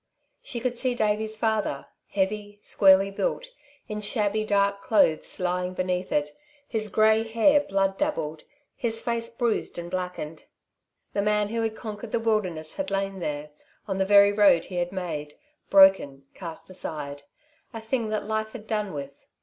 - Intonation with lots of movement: No, average, 3.3 semitones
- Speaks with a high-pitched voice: Yes, high, 205 Hz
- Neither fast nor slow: Yes, average, 160 wpm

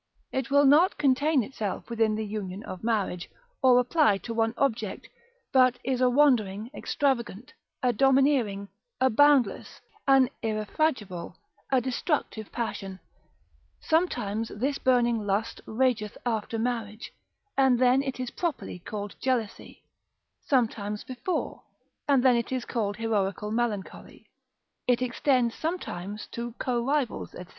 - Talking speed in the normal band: No, slow, 130 wpm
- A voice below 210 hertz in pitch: No, high, 240 Hz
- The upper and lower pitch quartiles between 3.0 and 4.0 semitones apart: Yes, average, 3.7 semitones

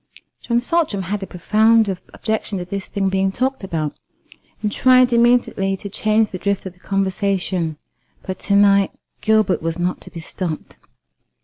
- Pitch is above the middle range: Yes, high, 200 Hz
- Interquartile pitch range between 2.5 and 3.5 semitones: Yes, average, 2.9 semitones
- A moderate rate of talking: Yes, average, 165 wpm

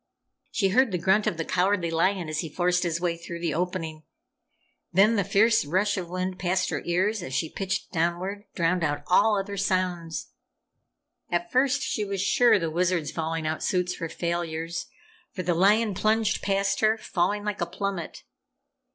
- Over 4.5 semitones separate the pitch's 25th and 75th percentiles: No, average, 3.0 semitones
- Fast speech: No, average, 175 wpm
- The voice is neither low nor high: Yes, medium, 180 Hz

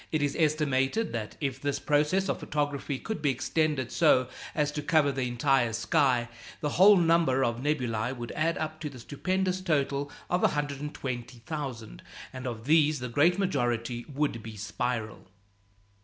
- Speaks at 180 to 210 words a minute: No, average, 155 wpm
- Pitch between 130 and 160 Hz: Yes, medium, 140 Hz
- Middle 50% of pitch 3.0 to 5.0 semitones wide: Yes, average, 4.1 semitones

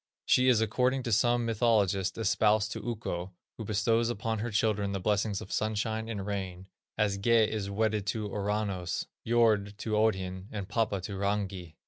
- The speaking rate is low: No, average, 165 wpm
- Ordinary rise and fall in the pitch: No, narrow, 2.2 semitones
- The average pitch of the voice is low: Yes, low, 105 Hz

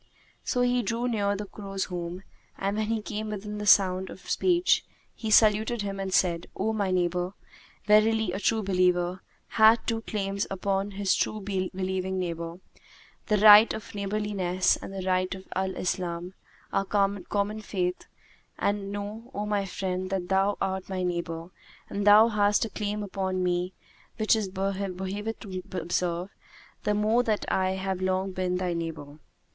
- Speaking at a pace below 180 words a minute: Yes, average, 160 wpm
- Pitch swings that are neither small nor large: No, narrow, 2.2 semitones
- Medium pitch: No, high, 195 Hz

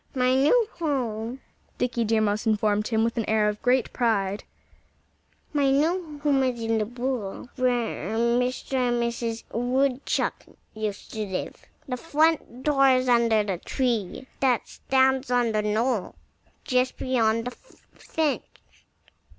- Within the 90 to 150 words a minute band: Yes, average, 140 wpm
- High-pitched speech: Yes, high, 245 Hz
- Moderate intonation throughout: Yes, average, 3.1 semitones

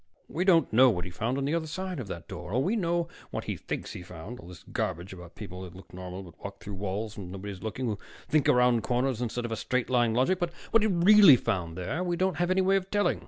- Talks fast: Yes, fast, 265 wpm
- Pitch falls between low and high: No, low, 120 Hz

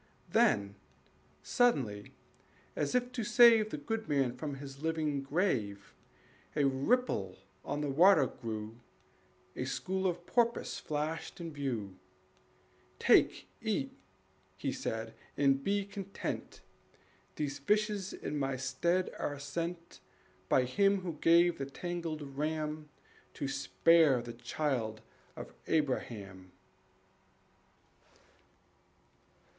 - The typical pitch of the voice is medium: Yes, medium, 150 Hz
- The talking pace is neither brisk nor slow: No, slow, 105 wpm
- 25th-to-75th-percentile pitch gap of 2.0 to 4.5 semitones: No, wide, 5.5 semitones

